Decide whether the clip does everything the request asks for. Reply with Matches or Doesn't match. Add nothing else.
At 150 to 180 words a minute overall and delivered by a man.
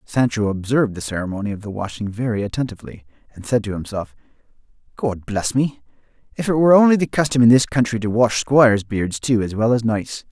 Doesn't match